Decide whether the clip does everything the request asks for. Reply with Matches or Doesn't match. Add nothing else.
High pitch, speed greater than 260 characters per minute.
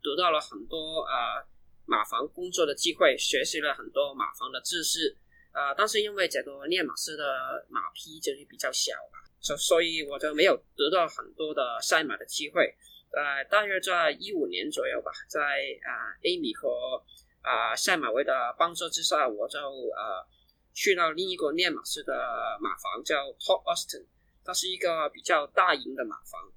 Matches